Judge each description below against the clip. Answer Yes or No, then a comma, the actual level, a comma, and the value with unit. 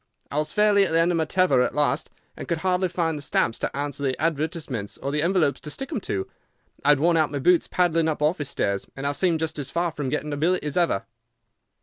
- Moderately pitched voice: Yes, medium, 155 Hz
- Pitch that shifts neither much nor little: Yes, average, 3.4 semitones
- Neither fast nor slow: No, fast, 255 wpm